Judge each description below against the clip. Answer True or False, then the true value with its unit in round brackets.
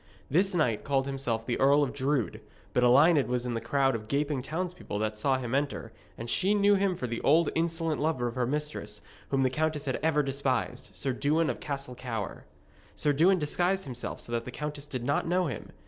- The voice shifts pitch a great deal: False (4.0 semitones)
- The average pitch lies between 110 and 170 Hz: True (140 Hz)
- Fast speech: True (210 wpm)